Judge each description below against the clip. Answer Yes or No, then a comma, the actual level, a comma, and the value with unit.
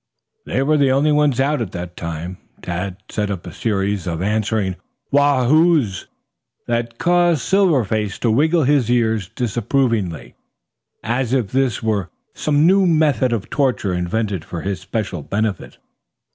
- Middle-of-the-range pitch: No, low, 115 Hz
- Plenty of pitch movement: Yes, wide, 6.3 semitones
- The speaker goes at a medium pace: Yes, average, 150 wpm